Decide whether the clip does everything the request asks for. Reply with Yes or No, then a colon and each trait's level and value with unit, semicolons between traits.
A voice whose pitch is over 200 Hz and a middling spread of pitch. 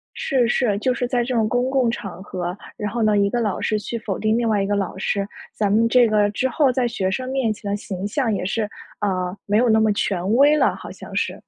Yes: high, 215 Hz; average, 3.3 semitones